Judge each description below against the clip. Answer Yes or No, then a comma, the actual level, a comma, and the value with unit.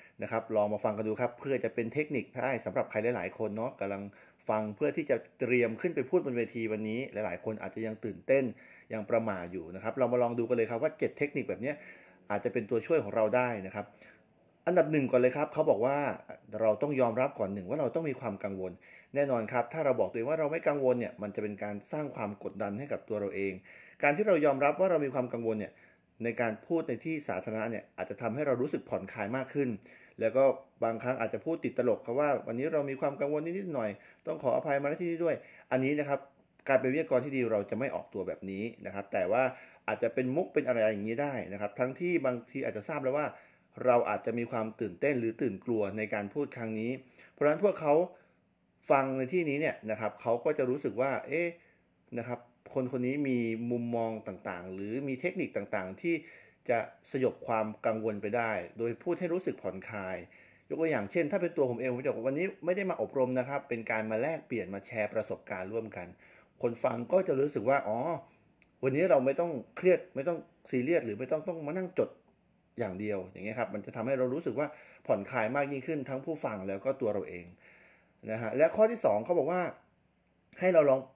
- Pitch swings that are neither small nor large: Yes, average, 4.9 semitones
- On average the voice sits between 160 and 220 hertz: No, low, 120 Hz